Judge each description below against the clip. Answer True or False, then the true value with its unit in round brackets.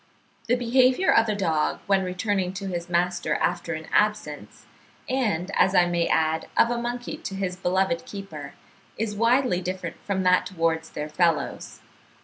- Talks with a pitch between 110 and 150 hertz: False (185 Hz)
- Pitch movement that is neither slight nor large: True (3.8 semitones)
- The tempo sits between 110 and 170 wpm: True (160 wpm)